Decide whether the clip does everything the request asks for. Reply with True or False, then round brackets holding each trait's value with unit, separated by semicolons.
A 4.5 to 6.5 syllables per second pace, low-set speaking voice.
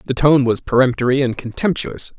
True (5.5 syllables/s; 130 Hz)